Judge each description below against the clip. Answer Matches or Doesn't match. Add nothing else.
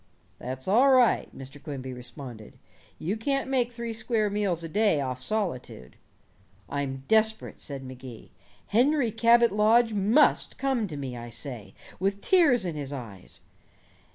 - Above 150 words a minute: Doesn't match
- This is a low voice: Doesn't match